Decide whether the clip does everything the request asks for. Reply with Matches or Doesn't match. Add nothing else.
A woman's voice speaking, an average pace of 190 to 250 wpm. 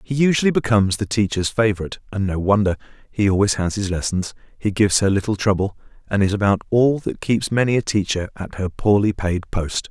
Doesn't match